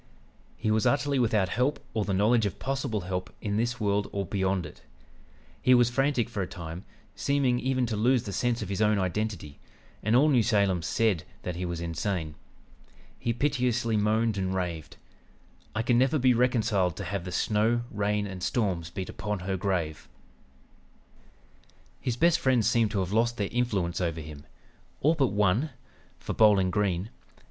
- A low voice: Yes, low, 105 Hz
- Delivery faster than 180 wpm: No, average, 175 wpm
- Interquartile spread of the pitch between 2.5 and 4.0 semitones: No, average, 4.4 semitones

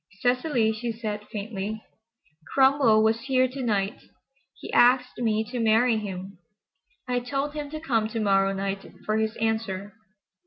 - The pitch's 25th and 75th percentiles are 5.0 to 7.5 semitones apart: No, average, 3.2 semitones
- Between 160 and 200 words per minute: No, average, 150 wpm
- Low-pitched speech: No, high, 225 Hz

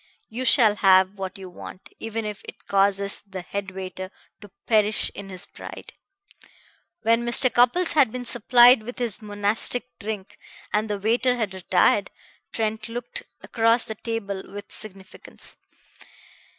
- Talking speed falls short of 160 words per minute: Yes, average, 145 wpm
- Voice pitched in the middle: No, high, 215 Hz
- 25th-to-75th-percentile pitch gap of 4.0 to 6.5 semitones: No, average, 3.1 semitones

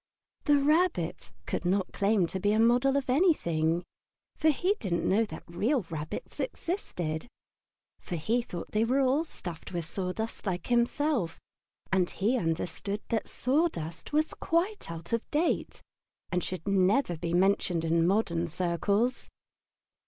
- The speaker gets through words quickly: No, average, 140 wpm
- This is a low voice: No, high, 200 Hz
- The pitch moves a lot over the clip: Yes, wide, 7.2 semitones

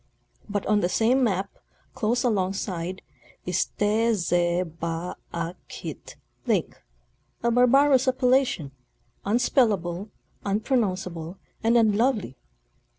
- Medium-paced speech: No, slow, 105 wpm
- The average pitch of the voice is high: Yes, high, 205 Hz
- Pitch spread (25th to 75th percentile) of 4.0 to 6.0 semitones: Yes, average, 5.1 semitones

